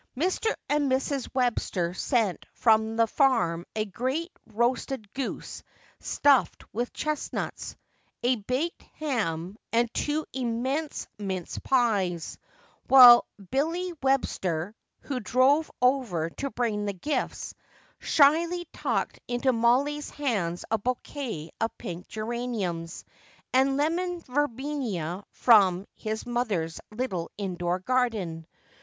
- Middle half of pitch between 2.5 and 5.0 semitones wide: No, wide, 5.6 semitones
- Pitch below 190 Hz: No, high, 240 Hz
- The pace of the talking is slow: Yes, slow, 110 wpm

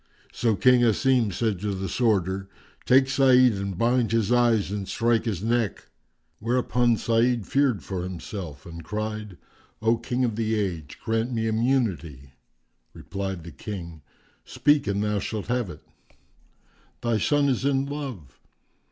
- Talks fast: No, average, 145 wpm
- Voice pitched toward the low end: Yes, low, 110 Hz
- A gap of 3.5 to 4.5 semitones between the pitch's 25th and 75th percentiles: Yes, average, 4.1 semitones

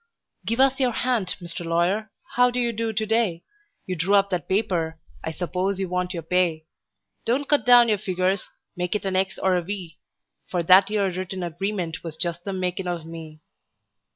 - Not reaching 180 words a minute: No, average, 195 wpm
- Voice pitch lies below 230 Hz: Yes, medium, 185 Hz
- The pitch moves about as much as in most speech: Yes, average, 3.5 semitones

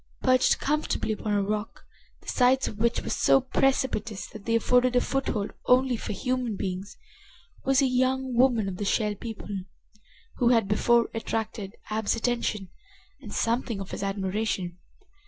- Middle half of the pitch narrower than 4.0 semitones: Yes, average, 3.5 semitones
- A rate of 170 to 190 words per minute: No, average, 155 wpm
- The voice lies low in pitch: No, high, 225 Hz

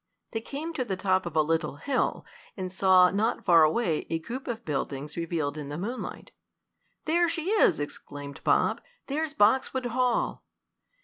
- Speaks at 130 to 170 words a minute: Yes, average, 165 wpm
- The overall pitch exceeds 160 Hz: Yes, high, 190 Hz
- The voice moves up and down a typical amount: No, wide, 8.3 semitones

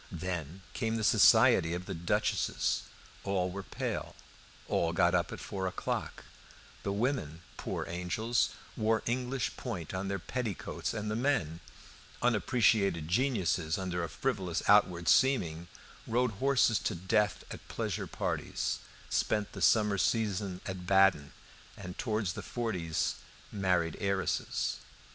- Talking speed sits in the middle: No, slow, 130 wpm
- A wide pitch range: No, average, 4.2 semitones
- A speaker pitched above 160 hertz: No, very low, 95 Hz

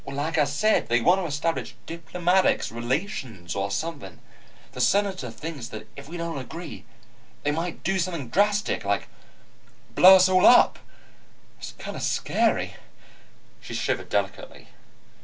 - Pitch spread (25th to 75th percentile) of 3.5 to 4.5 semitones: No, wide, 5.6 semitones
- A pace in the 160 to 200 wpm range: No, average, 140 wpm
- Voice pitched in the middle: Yes, medium, 165 Hz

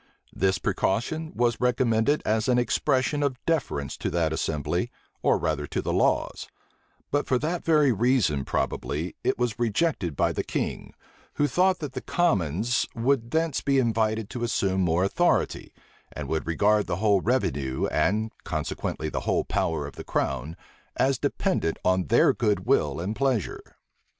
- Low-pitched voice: Yes, low, 110 Hz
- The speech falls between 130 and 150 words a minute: No, average, 160 wpm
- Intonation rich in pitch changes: Yes, wide, 7.3 semitones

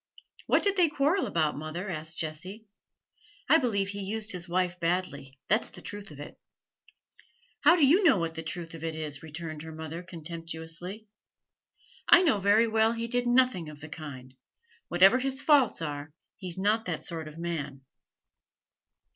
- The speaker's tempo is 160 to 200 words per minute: Yes, average, 170 wpm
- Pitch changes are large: Yes, wide, 5.8 semitones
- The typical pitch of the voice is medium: Yes, medium, 175 Hz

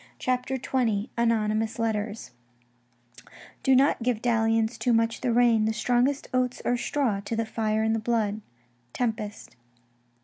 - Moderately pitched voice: No, high, 230 Hz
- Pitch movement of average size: No, narrow, 2.1 semitones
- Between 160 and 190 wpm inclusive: No, average, 150 wpm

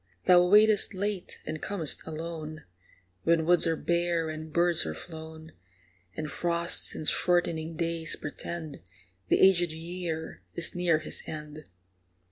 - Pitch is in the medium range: Yes, medium, 165 Hz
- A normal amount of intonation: No, narrow, 1.9 semitones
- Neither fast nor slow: No, slow, 130 wpm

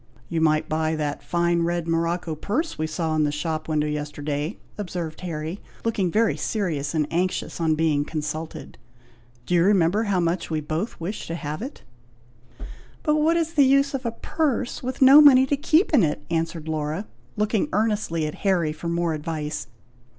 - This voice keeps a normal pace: Yes, average, 180 wpm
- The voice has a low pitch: No, medium, 170 Hz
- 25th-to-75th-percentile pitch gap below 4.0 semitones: No, wide, 5.5 semitones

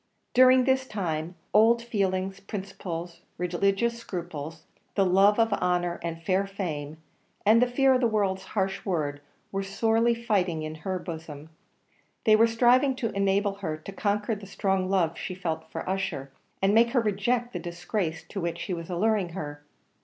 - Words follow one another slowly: No, average, 170 wpm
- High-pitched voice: Yes, high, 195 Hz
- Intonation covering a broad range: No, average, 4.3 semitones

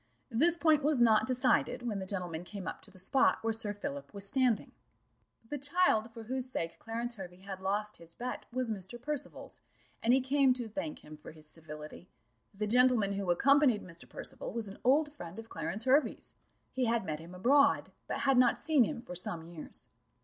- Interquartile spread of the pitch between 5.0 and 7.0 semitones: Yes, wide, 5.6 semitones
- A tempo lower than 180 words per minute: No, average, 200 wpm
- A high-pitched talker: Yes, high, 225 Hz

